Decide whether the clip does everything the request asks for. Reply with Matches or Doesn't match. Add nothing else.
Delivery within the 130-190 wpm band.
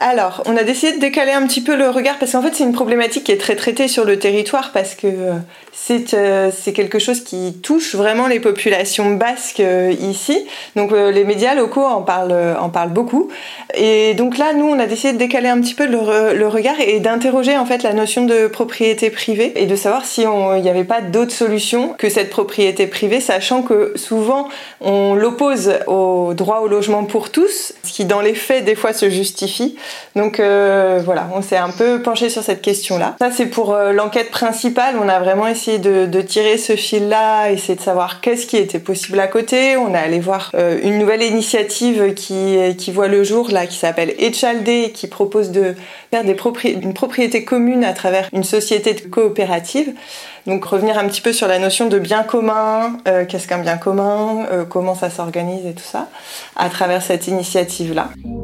Doesn't match